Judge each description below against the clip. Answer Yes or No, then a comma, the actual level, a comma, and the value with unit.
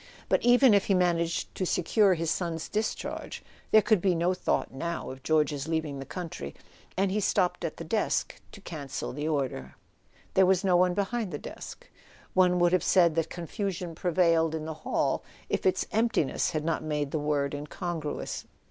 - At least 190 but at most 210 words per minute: Yes, average, 200 wpm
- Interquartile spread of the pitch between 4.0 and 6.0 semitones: No, average, 3.4 semitones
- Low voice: No, medium, 170 Hz